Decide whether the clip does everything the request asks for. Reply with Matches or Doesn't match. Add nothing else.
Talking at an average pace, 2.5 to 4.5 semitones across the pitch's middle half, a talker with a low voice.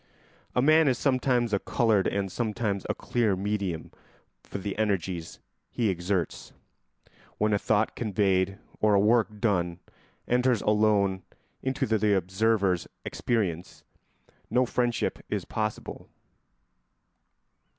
Doesn't match